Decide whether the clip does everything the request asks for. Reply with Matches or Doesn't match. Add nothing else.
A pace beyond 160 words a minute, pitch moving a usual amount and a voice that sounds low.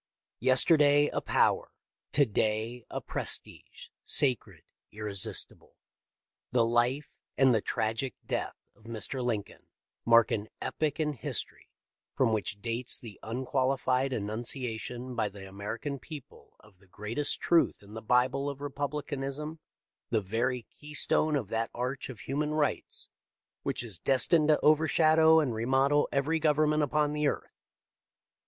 Doesn't match